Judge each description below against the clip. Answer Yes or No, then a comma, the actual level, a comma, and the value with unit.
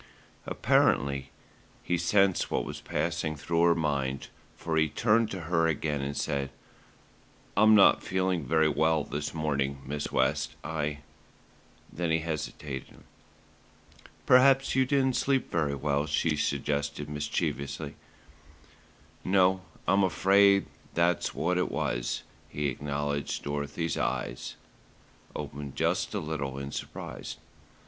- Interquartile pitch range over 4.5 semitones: No, average, 3.9 semitones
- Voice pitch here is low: Yes, very low, 75 Hz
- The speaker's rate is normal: No, slow, 125 wpm